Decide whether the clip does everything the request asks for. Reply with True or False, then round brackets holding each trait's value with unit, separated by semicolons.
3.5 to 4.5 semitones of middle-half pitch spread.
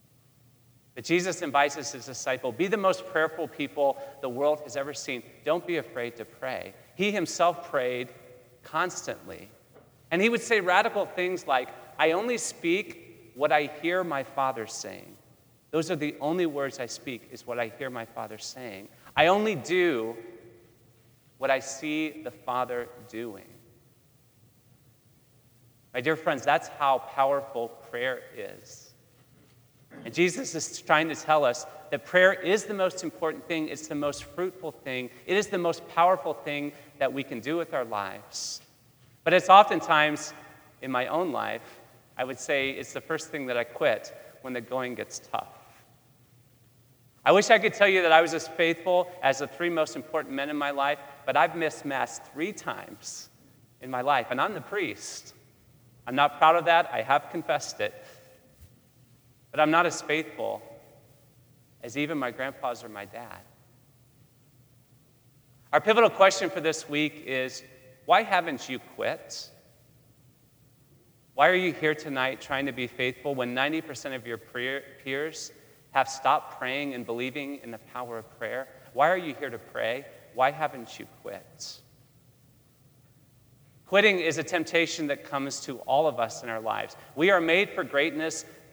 True (4.0 semitones)